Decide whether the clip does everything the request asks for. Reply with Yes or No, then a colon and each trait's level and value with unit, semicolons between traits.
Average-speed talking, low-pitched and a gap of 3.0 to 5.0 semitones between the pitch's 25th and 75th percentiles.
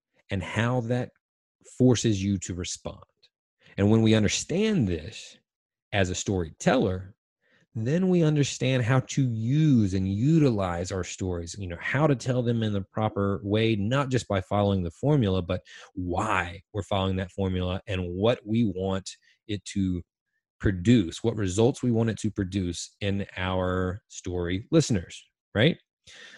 Yes: average, 150 wpm; low, 100 Hz; average, 4.4 semitones